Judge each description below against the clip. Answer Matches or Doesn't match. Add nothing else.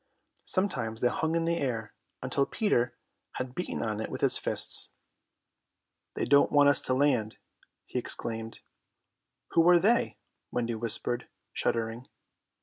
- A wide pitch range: Matches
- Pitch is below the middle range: Matches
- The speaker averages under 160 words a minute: Matches